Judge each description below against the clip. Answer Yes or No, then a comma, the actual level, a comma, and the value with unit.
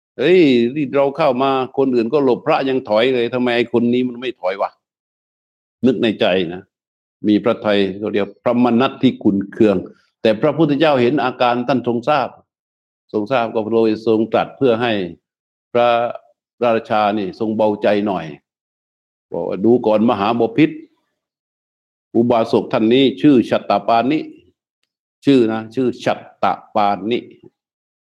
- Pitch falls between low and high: No, low, 120 Hz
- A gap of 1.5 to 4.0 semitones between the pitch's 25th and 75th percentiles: Yes, average, 3.4 semitones